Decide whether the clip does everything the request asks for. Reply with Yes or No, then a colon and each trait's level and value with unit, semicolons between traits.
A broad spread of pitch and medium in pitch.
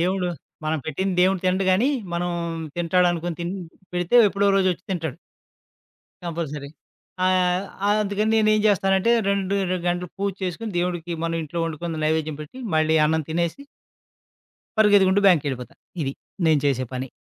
No: average, 3.3 semitones; medium, 175 Hz